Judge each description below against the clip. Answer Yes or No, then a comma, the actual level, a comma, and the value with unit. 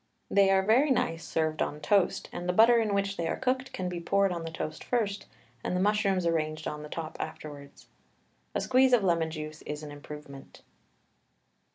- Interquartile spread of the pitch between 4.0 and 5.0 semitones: Yes, average, 4.6 semitones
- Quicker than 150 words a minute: Yes, average, 195 wpm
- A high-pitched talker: No, medium, 175 Hz